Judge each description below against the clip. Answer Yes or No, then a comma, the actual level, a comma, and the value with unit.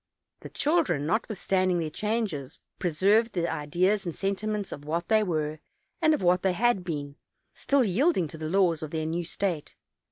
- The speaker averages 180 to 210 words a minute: Yes, average, 185 wpm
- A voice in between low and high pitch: Yes, medium, 180 Hz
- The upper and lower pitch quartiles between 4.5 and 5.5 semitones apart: Yes, average, 5.1 semitones